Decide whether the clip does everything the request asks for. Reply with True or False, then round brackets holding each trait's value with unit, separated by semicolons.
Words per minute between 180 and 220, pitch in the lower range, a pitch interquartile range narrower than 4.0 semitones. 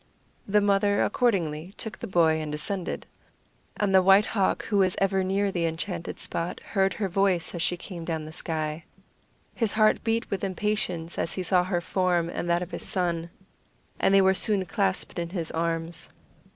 False (185 wpm; 185 Hz; 2.7 semitones)